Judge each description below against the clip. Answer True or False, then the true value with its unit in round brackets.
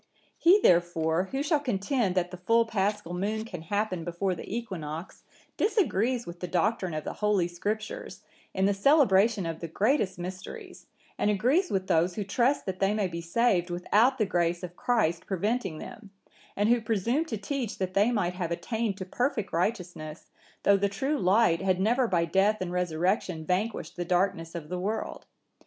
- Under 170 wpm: False (180 wpm)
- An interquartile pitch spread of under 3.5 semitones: False (4.1 semitones)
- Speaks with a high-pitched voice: True (195 Hz)